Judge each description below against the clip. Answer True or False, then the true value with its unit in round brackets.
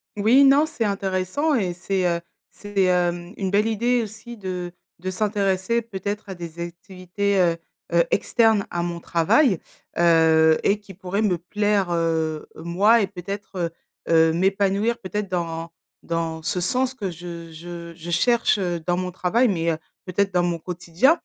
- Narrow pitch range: False (3.3 semitones)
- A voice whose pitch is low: False (185 Hz)